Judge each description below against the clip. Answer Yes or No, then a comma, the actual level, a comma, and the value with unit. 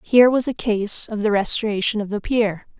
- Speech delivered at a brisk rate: Yes, fast, 215 wpm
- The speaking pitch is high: Yes, high, 215 Hz